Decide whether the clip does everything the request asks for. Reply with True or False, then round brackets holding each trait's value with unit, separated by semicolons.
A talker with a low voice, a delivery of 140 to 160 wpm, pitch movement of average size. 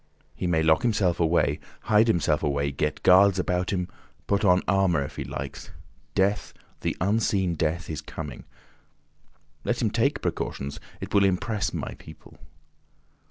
True (90 Hz; 145 wpm; 4.1 semitones)